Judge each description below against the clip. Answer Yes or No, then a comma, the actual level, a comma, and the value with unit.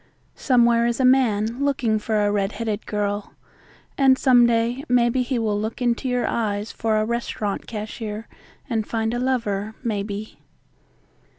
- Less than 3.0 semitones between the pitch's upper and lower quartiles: Yes, narrow, 2.6 semitones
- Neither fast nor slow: Yes, average, 155 wpm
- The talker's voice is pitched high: Yes, high, 230 Hz